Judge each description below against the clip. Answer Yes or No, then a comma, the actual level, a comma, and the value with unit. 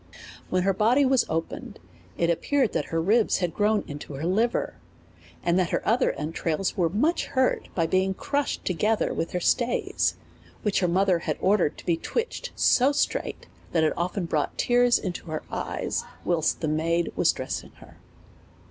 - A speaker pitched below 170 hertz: No, medium, 185 Hz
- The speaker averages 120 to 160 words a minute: No, average, 180 wpm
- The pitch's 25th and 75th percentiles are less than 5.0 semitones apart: No, wide, 5.4 semitones